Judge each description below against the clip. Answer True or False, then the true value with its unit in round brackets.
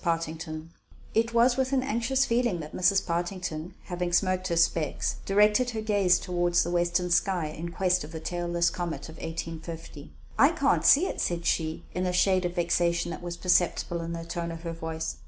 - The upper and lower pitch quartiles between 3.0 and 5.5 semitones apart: False (2.6 semitones)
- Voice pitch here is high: False (175 Hz)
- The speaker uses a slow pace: False (195 wpm)